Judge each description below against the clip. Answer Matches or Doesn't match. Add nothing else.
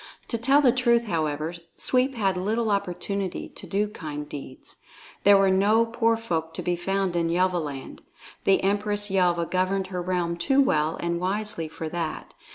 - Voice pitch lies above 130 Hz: Matches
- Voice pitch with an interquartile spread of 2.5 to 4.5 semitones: Matches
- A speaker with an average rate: Matches